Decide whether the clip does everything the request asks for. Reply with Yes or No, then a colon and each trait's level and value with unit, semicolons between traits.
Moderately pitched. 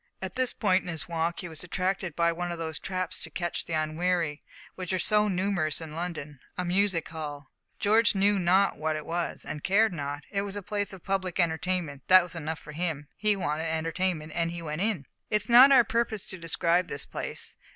Yes: medium, 175 Hz